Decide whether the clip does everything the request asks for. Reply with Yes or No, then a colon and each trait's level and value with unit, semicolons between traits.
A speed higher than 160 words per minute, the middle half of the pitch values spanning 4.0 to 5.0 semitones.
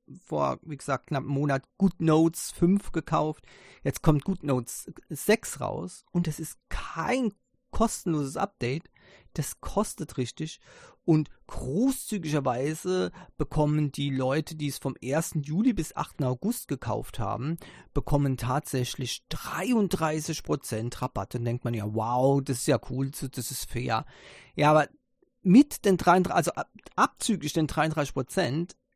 No: average, 135 wpm; average, 4.6 semitones